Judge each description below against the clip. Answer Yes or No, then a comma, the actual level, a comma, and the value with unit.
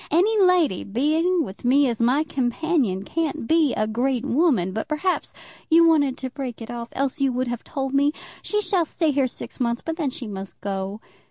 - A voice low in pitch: No, very high, 270 Hz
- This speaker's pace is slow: No, average, 200 wpm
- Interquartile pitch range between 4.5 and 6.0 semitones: Yes, average, 5.2 semitones